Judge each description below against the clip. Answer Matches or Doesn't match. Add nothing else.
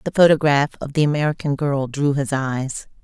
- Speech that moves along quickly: Doesn't match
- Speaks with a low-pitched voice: Doesn't match